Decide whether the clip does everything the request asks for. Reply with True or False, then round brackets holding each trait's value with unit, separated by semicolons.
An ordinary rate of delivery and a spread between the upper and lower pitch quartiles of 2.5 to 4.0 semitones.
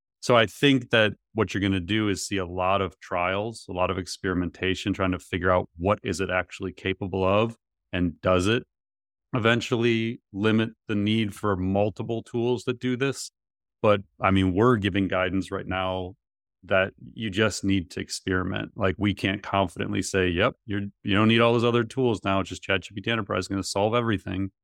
True (195 wpm; 3.0 semitones)